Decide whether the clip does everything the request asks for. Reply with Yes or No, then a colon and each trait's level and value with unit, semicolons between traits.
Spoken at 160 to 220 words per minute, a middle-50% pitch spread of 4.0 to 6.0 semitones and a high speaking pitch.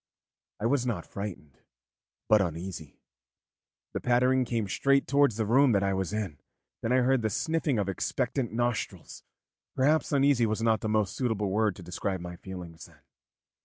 No: average, 165 wpm; average, 4.8 semitones; low, 110 Hz